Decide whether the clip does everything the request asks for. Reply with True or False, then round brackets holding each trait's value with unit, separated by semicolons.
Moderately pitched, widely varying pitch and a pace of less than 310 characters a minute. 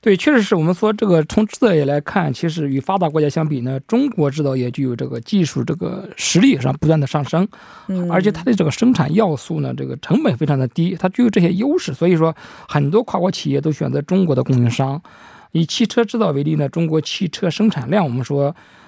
False (165 Hz; 5.9 semitones; 345 characters per minute)